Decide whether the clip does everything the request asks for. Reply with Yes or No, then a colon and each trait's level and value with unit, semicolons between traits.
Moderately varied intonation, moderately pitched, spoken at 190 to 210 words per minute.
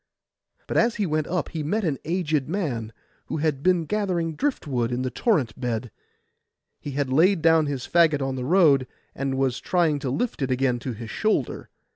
Yes: average, 5.0 semitones; medium, 150 Hz; average, 195 wpm